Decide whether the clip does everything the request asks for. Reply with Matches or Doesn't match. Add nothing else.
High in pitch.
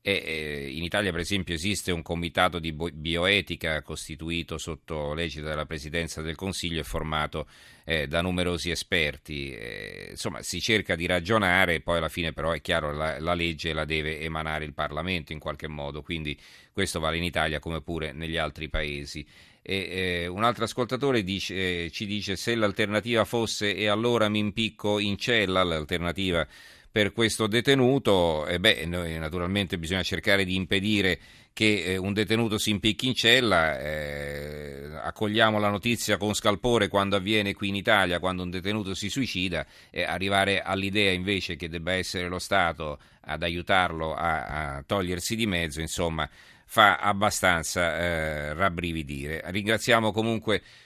Doesn't match